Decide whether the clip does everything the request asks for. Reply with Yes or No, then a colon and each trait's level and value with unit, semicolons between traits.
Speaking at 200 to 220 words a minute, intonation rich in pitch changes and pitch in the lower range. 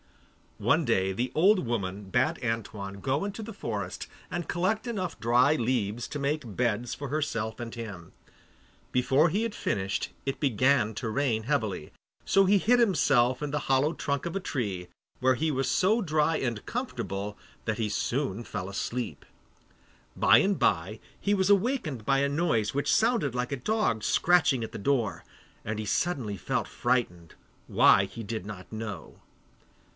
No: average, 170 wpm; wide, 6.4 semitones; low, 125 Hz